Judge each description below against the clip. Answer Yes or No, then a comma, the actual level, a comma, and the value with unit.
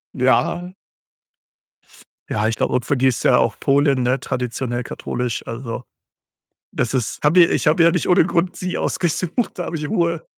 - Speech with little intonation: No, wide, 5.4 semitones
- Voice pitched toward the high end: No, medium, 140 Hz